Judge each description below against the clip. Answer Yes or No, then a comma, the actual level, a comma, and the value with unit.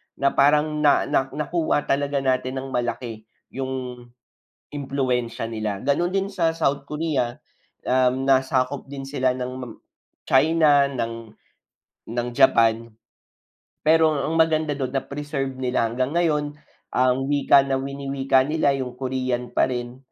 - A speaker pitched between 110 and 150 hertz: Yes, low, 135 Hz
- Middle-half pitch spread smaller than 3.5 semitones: Yes, narrow, 2.6 semitones